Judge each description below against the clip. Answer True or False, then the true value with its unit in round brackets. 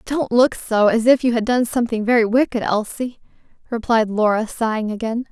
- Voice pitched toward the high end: True (230 Hz)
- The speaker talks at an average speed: True (170 wpm)